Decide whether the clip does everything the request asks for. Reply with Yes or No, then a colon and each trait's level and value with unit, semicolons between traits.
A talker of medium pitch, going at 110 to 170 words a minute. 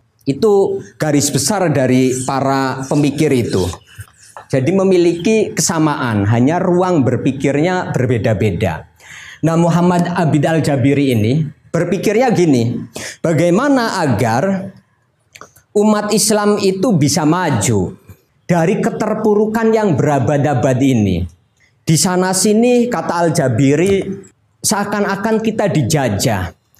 No: medium, 155 Hz; average, 90 wpm